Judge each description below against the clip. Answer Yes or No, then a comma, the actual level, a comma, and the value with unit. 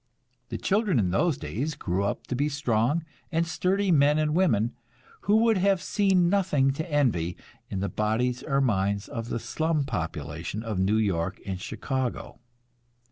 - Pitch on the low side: Yes, low, 130 Hz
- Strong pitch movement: Yes, wide, 8.2 semitones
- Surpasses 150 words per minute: Yes, average, 165 wpm